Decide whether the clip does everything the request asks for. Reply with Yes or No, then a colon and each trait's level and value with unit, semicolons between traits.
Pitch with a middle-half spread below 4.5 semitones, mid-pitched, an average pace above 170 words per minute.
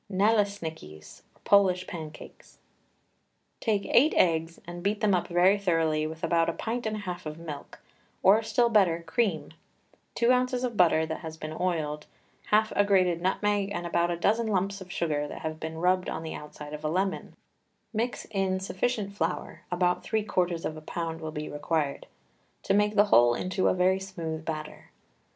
Yes: average, 4.1 semitones; medium, 180 Hz; average, 180 wpm